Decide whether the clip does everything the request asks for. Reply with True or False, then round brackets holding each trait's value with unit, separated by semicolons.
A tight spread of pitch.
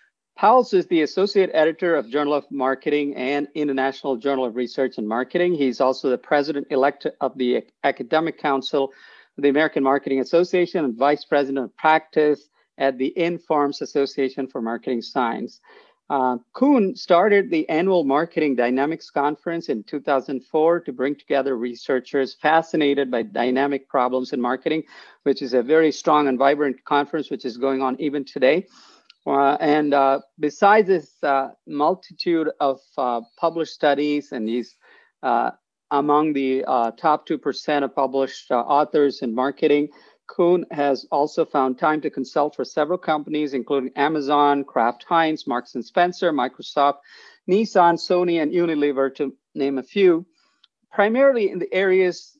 False (3.3 semitones)